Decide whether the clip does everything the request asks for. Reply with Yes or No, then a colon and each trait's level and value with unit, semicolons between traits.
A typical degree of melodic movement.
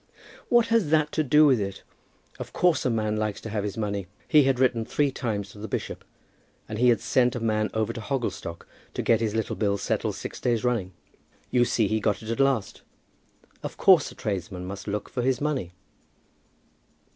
Yes: average, 4.0 semitones